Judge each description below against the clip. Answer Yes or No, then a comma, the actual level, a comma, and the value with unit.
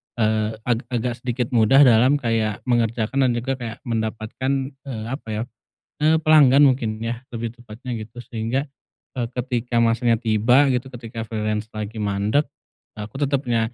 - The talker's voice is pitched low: Yes, low, 115 Hz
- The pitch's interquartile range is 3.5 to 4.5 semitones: No, average, 2.8 semitones